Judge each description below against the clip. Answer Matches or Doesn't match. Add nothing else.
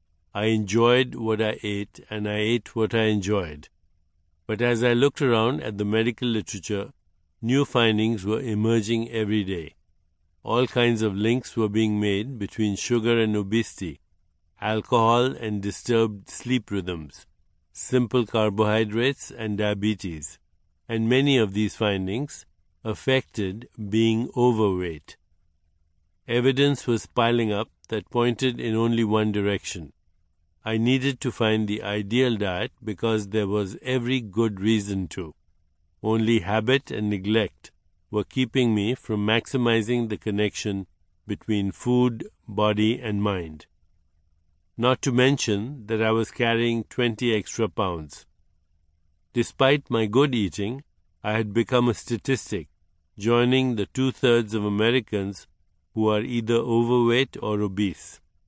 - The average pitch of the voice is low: Matches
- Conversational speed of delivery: Doesn't match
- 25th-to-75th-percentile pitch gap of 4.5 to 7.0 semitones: Doesn't match